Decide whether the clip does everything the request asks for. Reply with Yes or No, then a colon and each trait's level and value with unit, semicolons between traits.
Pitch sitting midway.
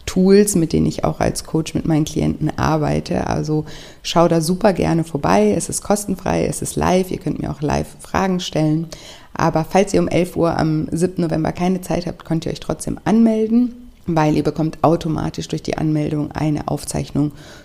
Yes: medium, 160 Hz